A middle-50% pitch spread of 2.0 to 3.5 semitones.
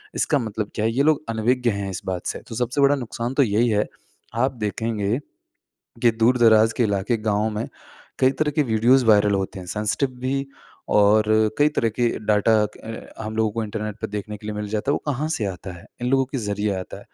Yes: average, 3.2 semitones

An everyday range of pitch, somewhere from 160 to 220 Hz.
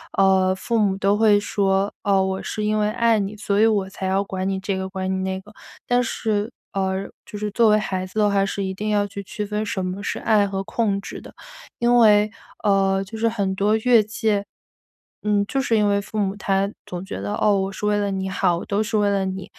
No: narrow, 1.8 semitones; high, 200 Hz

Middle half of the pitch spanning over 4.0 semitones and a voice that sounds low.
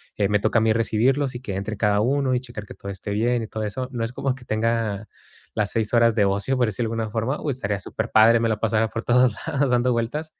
No: average, 2.8 semitones; low, 115 Hz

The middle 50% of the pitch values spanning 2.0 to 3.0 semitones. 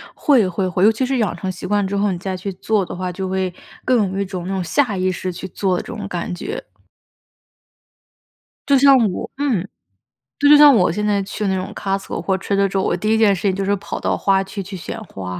Yes: narrow, 2.4 semitones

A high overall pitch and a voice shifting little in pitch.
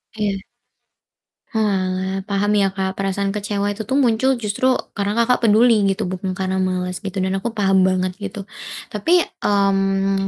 Yes: high, 200 Hz; narrow, 2.0 semitones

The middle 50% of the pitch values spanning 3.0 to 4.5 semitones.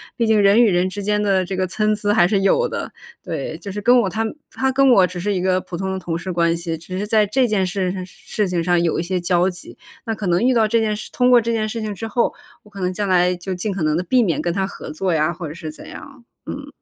Yes: average, 3.4 semitones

